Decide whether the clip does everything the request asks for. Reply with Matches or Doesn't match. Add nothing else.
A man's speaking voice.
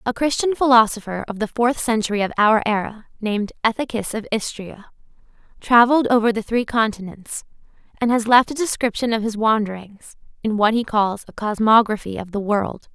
Doesn't match